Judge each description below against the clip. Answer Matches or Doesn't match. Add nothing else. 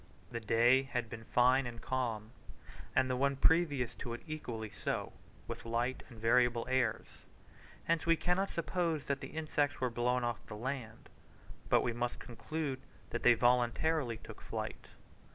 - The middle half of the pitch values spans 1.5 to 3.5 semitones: Matches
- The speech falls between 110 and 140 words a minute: Doesn't match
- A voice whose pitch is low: Matches